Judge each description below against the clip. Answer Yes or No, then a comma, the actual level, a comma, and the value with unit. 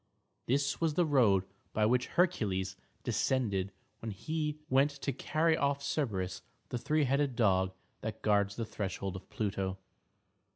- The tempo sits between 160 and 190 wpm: No, average, 140 wpm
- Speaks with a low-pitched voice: Yes, low, 120 Hz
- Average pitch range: No, wide, 6.3 semitones